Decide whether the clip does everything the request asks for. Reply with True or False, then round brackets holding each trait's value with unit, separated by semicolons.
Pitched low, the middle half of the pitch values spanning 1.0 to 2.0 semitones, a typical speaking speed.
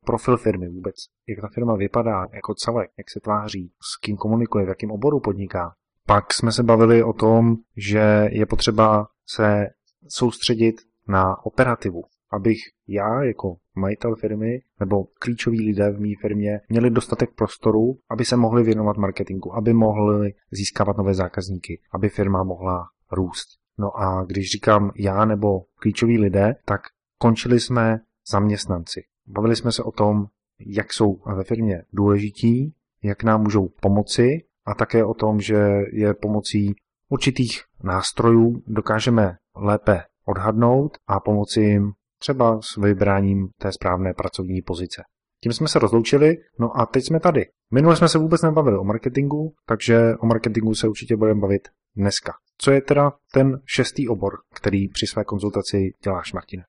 False (110 Hz; 2.6 semitones; 150 wpm)